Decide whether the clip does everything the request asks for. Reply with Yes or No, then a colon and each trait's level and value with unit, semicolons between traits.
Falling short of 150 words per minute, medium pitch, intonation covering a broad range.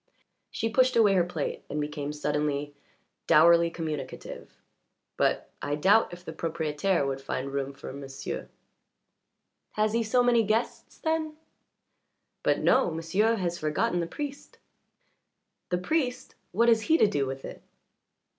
Yes: average, 140 wpm; medium, 170 Hz; wide, 7.3 semitones